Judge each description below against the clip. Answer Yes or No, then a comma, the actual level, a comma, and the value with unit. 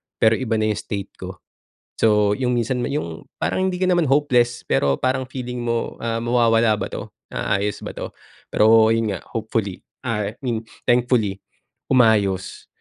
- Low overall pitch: Yes, low, 115 Hz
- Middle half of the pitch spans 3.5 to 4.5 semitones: No, average, 2.8 semitones